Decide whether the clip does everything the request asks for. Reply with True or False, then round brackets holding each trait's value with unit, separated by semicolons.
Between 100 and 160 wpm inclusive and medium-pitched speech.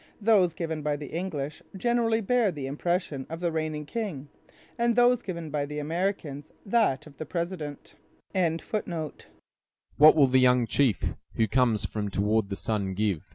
True (155 wpm; 155 Hz)